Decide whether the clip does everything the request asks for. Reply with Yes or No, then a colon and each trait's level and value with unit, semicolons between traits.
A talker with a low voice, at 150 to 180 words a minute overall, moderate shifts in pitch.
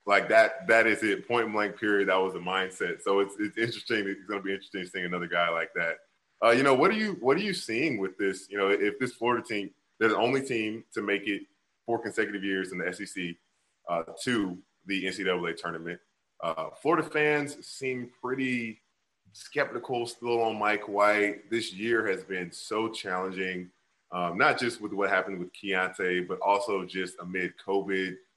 No: low, 100 Hz; average, 190 wpm; average, 3.3 semitones